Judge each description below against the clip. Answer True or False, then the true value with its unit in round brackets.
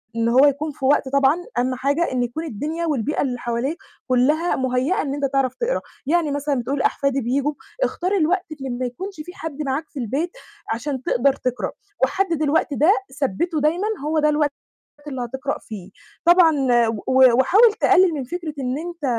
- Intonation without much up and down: False (3.9 semitones)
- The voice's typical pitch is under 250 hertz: False (285 Hz)